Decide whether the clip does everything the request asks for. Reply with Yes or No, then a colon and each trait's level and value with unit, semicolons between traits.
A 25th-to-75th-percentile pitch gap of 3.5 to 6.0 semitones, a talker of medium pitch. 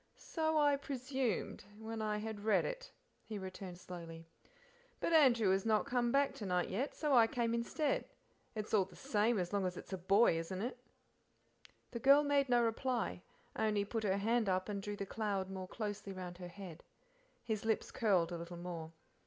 No: average, 4.3 semitones; high, 210 Hz